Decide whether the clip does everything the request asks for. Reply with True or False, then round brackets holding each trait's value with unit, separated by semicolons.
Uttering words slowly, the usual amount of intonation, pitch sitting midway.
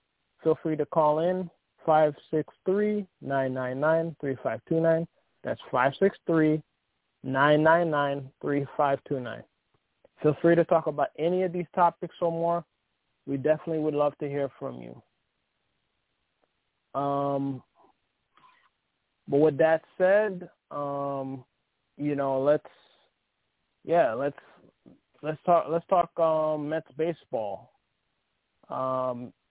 True (95 wpm; 3.2 semitones; 155 Hz)